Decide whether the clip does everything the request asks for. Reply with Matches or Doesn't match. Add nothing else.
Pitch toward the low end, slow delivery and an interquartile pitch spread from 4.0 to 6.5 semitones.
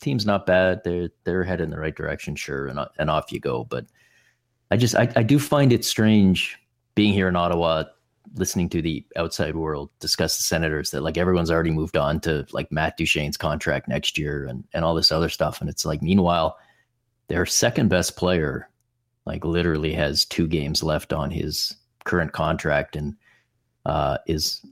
Doesn't match